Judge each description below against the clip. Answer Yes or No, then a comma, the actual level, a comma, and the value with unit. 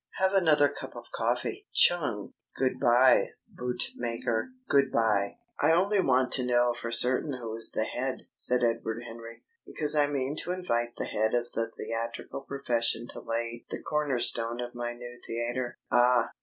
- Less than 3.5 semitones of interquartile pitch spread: Yes, average, 2.8 semitones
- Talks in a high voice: No, low, 120 Hz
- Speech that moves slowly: No, average, 170 wpm